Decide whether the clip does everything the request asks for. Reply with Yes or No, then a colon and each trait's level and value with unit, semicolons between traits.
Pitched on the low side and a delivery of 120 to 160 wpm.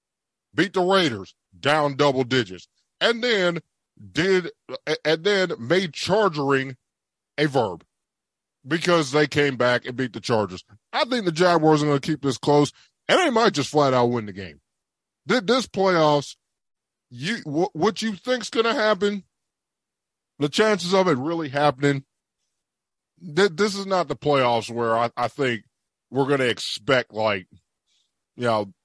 No: medium, 145 Hz; average, 150 wpm